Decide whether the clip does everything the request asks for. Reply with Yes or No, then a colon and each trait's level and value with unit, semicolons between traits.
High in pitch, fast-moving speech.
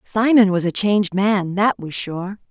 No: high, 200 Hz; average, 190 wpm